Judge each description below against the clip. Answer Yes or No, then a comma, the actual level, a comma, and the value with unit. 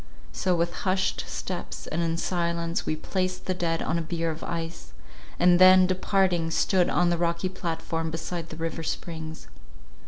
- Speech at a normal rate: Yes, average, 165 wpm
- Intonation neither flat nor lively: No, narrow, 1.9 semitones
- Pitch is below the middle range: No, medium, 170 Hz